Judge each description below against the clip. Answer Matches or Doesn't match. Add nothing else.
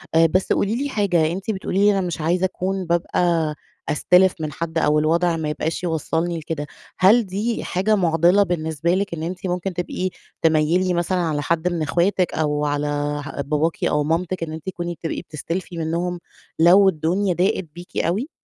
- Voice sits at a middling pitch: Matches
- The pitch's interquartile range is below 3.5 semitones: Matches